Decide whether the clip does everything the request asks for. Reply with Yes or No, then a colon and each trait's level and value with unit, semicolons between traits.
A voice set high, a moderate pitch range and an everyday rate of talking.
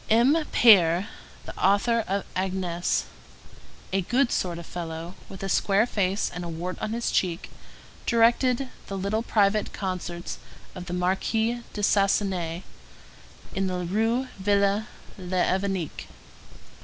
No: high, 195 Hz; average, 3.5 semitones; slow, 130 wpm